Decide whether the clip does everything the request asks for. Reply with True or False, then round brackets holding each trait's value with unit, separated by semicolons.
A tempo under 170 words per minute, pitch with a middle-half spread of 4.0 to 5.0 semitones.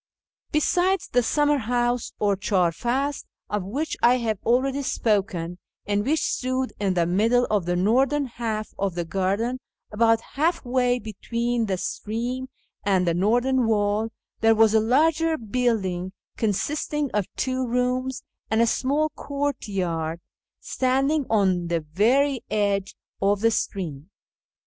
True (140 wpm; 4.6 semitones)